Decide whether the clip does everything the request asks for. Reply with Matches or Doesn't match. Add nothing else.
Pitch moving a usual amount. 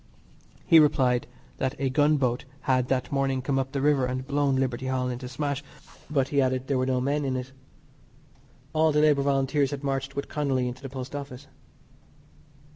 Doesn't match